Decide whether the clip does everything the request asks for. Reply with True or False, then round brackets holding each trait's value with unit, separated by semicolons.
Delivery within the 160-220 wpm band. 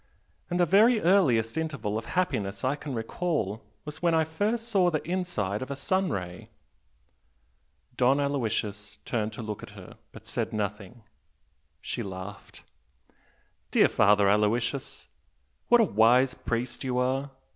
False (145 wpm)